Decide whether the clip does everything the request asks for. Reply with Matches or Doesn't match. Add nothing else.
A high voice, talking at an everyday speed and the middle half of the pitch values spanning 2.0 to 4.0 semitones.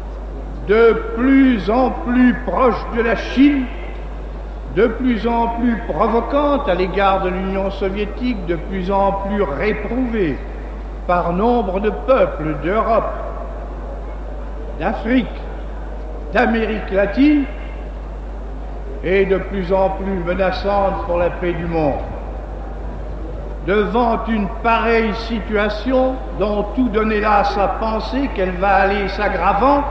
Doesn't match